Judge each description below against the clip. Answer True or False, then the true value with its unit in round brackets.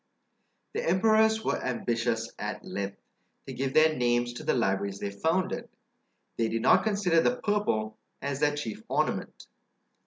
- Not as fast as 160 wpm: True (150 wpm)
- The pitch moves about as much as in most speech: False (8.6 semitones)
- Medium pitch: False (130 Hz)